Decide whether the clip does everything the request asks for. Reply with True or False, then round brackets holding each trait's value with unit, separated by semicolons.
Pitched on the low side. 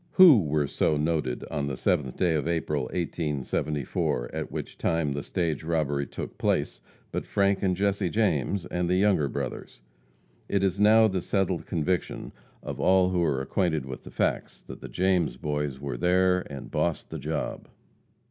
True (85 Hz)